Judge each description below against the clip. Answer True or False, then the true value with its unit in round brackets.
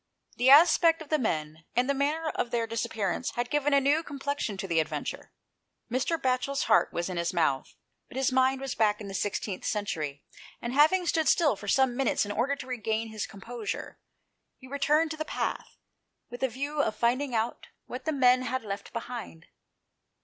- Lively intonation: False (4.9 semitones)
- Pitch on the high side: True (250 Hz)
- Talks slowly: False (195 wpm)